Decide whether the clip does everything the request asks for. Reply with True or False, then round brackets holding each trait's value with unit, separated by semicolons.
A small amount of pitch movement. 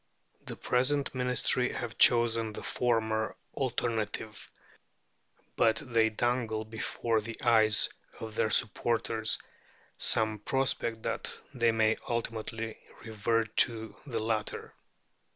True (1.4 semitones)